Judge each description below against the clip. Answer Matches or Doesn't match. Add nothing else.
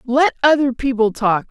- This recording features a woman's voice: Matches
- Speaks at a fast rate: Doesn't match